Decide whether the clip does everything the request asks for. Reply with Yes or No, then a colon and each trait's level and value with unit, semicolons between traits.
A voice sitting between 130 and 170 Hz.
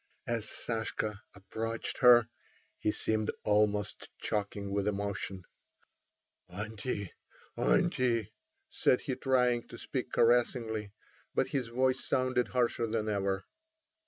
No: low, 110 Hz